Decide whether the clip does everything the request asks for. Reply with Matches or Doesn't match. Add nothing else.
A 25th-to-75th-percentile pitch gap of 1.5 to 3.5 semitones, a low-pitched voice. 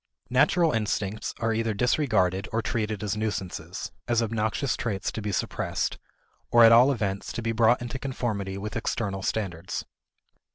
Matches